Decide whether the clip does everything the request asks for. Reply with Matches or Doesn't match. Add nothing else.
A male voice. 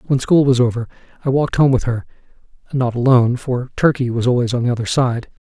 Matches